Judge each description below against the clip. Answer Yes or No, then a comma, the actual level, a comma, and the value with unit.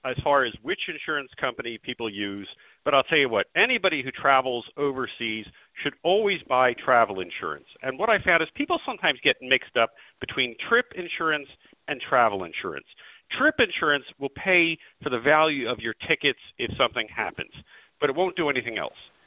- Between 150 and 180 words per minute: Yes, average, 175 wpm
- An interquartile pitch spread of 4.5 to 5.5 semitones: Yes, average, 5.1 semitones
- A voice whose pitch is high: No, medium, 140 Hz